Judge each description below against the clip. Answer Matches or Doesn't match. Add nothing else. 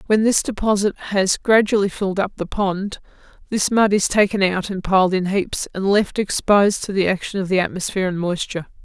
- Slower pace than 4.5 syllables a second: Doesn't match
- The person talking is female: Matches